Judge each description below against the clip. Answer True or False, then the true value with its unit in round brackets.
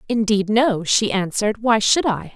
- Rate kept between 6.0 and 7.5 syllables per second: False (4.6 syllables/s)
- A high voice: True (215 Hz)